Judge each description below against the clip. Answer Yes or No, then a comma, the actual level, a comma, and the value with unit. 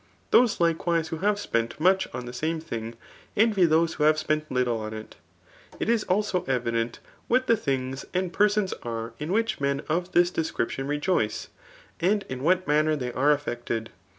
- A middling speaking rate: Yes, average, 170 wpm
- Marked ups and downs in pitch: Yes, wide, 6.5 semitones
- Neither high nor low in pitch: Yes, medium, 155 Hz